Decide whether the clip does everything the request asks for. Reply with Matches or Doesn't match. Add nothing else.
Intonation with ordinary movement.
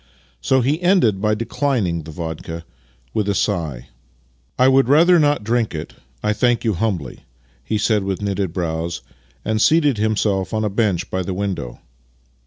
Doesn't match